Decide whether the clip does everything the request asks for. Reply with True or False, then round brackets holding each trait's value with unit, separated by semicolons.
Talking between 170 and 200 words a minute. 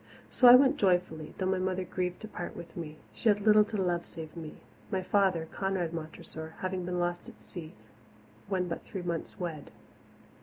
True (190 wpm)